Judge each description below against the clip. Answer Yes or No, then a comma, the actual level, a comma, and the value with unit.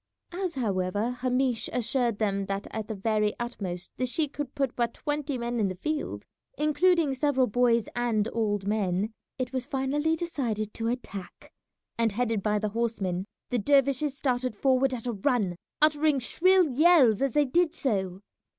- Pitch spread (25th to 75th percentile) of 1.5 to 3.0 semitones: No, average, 4.8 semitones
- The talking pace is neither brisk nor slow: Yes, average, 165 wpm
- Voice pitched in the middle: No, high, 245 Hz